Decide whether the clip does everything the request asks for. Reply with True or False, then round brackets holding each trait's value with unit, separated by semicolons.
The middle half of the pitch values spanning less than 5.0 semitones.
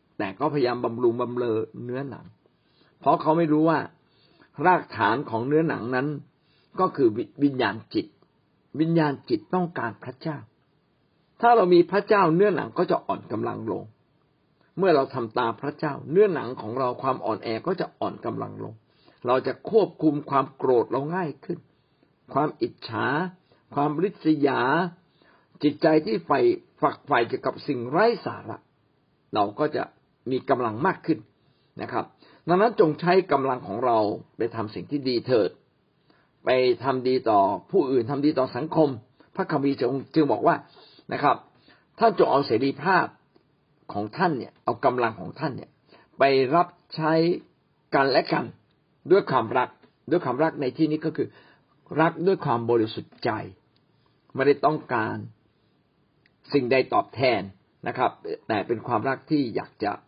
True (4.5 semitones)